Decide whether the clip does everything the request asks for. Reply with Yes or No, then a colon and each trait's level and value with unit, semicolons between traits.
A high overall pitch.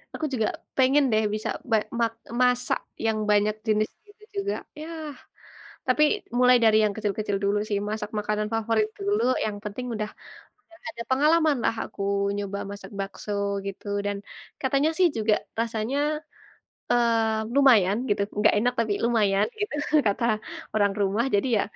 Yes: high, 220 Hz